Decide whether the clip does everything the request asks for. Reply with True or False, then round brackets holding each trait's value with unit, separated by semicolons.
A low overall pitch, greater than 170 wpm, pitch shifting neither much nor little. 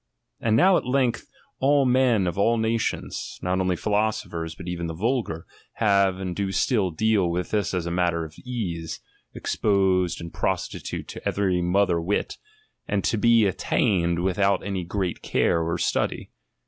False (95 Hz; 165 wpm; 4.0 semitones)